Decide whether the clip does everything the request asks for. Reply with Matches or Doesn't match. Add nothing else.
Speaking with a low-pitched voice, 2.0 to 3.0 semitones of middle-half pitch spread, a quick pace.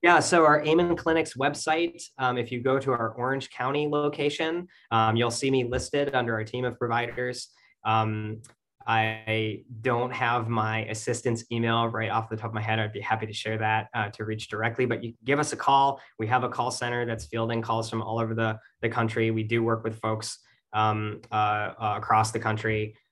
Matches